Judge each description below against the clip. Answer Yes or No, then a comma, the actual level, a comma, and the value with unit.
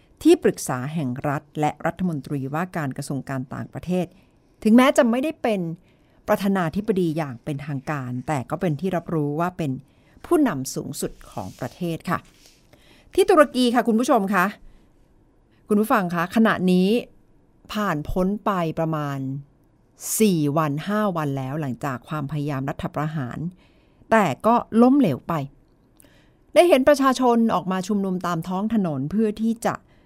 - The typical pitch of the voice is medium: Yes, medium, 175 Hz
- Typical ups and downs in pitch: No, wide, 6.5 semitones